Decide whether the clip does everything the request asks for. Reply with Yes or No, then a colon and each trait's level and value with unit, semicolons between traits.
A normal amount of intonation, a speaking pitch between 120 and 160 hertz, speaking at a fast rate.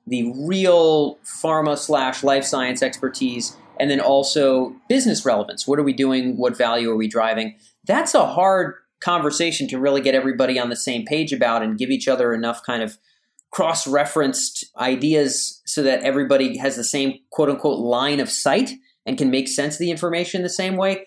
No: average, 3.5 semitones; low, 135 Hz; average, 185 wpm